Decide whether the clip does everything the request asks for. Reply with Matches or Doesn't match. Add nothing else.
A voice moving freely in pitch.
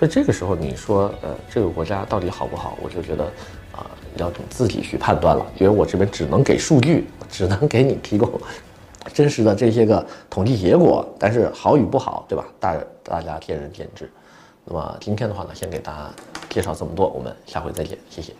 Doesn't match